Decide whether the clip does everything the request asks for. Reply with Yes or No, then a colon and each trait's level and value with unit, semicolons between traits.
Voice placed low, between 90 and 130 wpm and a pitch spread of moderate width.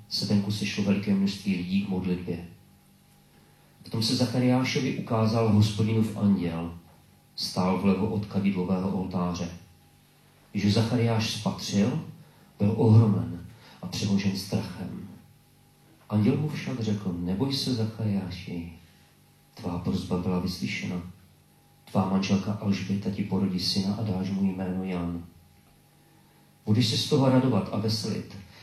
Yes: low, 100 Hz; average, 120 wpm; average, 3.4 semitones